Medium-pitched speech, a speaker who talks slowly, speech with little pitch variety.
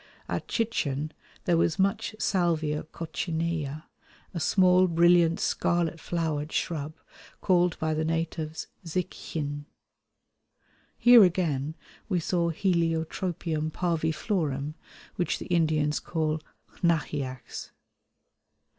Yes: medium, 165 Hz; slow, 95 wpm; narrow, 2.2 semitones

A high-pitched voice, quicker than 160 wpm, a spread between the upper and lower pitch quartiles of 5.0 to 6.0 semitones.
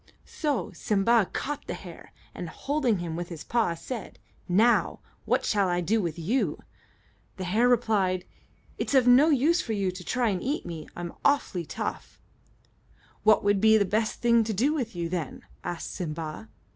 Yes: high, 215 Hz; average, 175 wpm; wide, 5.5 semitones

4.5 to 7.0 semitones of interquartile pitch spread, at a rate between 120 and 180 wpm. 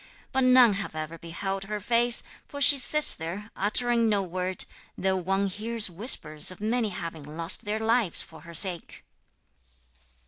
Yes: average, 5.2 semitones; average, 160 wpm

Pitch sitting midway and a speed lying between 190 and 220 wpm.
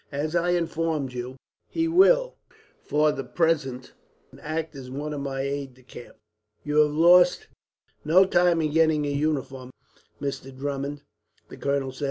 No: medium, 150 Hz; average, 155 wpm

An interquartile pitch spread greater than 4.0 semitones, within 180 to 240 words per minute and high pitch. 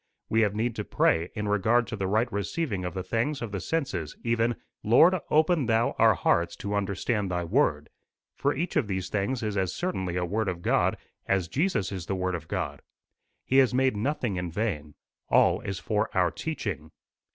No: average, 4.6 semitones; average, 195 wpm; low, 105 Hz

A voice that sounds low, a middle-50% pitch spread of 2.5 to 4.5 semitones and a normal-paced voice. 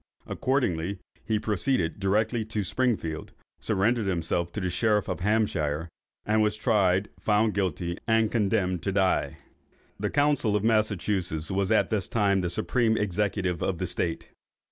Yes: low, 100 Hz; average, 3.3 semitones; average, 145 wpm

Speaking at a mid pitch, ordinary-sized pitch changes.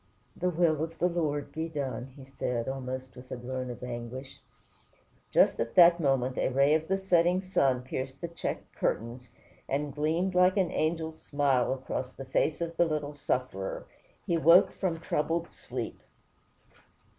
Yes: medium, 145 Hz; average, 4.4 semitones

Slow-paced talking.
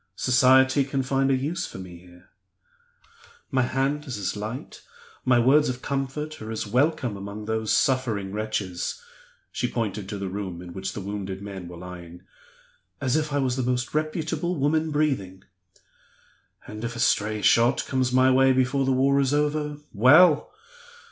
No: average, 170 wpm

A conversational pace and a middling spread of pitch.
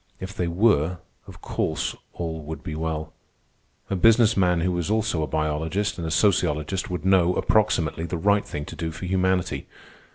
Yes: average, 175 wpm; average, 3.3 semitones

